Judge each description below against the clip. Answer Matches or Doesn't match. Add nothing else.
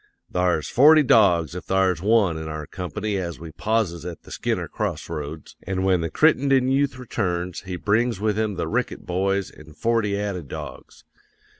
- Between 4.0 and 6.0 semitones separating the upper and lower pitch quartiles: Matches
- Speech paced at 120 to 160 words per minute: Doesn't match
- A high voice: Doesn't match